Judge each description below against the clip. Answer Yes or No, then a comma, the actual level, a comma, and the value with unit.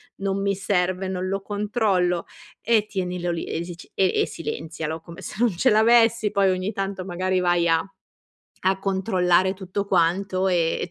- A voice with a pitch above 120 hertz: Yes, high, 190 Hz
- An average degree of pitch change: No, narrow, 2.0 semitones